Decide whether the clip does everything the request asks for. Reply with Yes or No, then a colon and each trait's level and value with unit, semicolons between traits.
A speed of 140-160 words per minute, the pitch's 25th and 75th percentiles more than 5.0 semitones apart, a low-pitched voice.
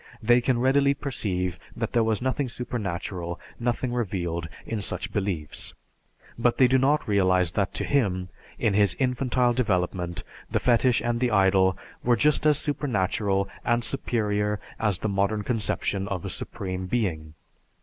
No: average, 150 wpm; average, 4.7 semitones; low, 105 Hz